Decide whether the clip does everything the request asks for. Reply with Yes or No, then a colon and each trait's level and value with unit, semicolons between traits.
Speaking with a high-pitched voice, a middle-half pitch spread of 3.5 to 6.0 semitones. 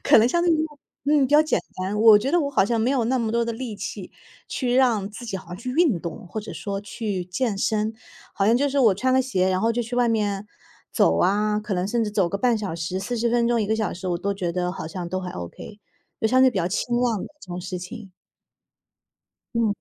Yes: high, 215 Hz; average, 4.2 semitones